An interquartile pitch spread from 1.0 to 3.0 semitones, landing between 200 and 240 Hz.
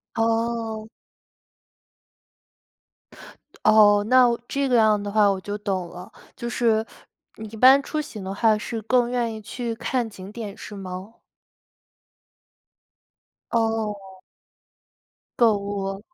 Yes: narrow, 2.4 semitones; high, 220 Hz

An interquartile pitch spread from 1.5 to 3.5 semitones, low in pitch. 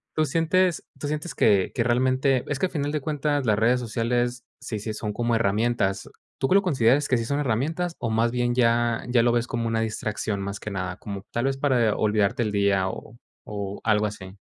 No: average, 4.0 semitones; low, 120 Hz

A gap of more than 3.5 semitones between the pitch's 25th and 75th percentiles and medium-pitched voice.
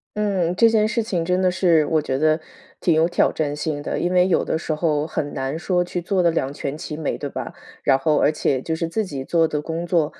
No: average, 3.0 semitones; medium, 165 Hz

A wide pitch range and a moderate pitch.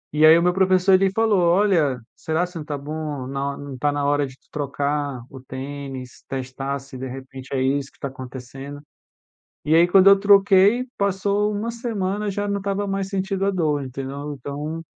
Yes: wide, 6.0 semitones; medium, 150 Hz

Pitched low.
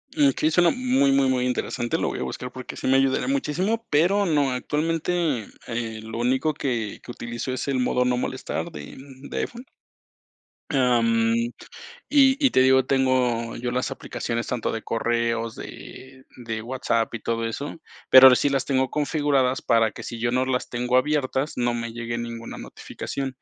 Yes: low, 130 Hz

